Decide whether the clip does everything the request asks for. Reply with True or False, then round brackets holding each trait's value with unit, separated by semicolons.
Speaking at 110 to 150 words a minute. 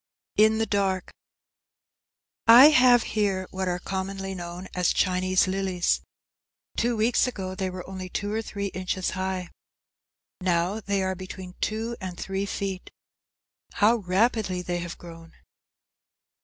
True (140 wpm)